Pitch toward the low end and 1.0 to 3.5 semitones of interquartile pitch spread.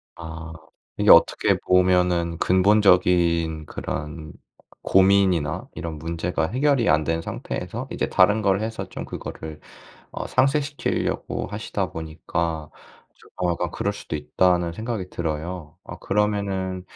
Yes: very low, 90 Hz; average, 3.2 semitones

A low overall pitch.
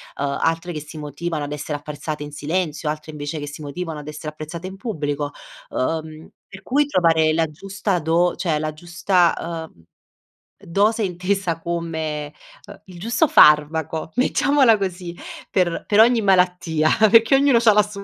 No: medium, 165 Hz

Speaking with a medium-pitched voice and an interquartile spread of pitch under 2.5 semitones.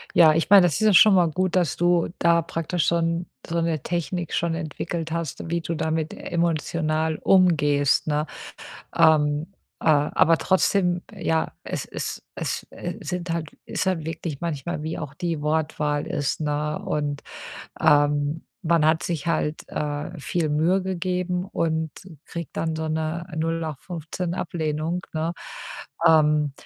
Yes: medium, 160 Hz; narrow, 2.1 semitones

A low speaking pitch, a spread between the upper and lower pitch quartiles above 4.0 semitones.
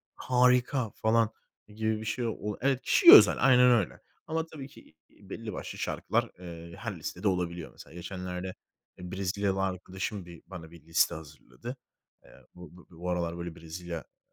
Yes: very low, 95 Hz; average, 4.8 semitones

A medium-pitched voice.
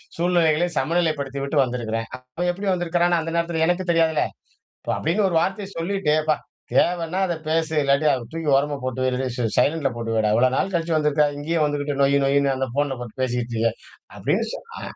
Yes: medium, 150 Hz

